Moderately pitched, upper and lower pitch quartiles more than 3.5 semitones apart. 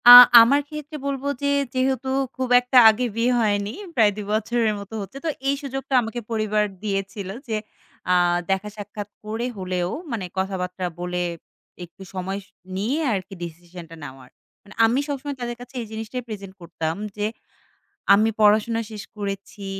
No: high, 215 Hz; average, 3.9 semitones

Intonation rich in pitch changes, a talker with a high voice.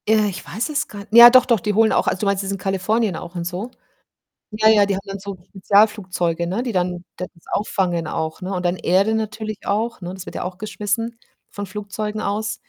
No: average, 2.9 semitones; high, 200 Hz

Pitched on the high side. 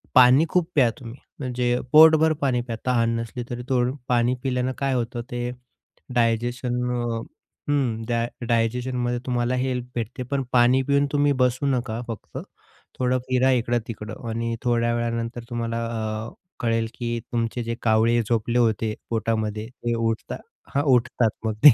No: low, 120 Hz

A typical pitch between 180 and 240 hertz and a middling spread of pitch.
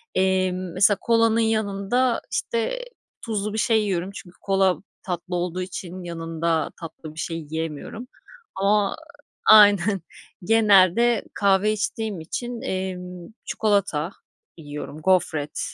Yes: high, 190 Hz; average, 3.8 semitones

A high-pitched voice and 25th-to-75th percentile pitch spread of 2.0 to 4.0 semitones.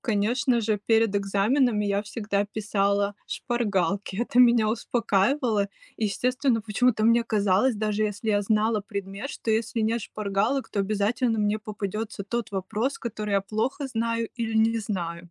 Yes: high, 215 Hz; narrow, 2.4 semitones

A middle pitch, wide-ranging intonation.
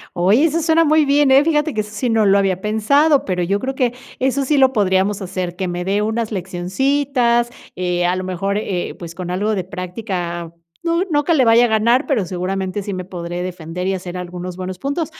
No: high, 200 Hz; wide, 6.4 semitones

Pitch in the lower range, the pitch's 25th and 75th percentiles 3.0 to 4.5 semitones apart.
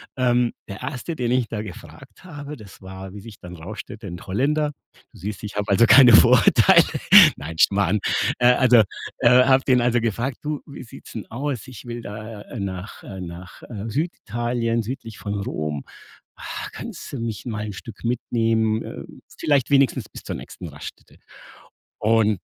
Yes: low, 115 Hz; average, 3.6 semitones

